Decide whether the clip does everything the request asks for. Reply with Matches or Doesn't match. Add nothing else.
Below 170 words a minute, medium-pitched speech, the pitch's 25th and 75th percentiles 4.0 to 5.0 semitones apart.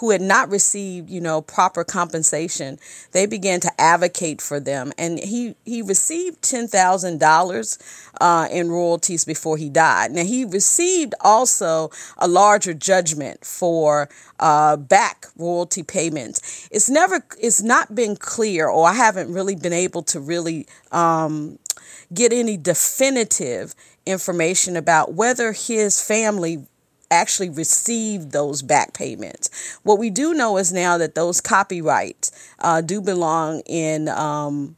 Matches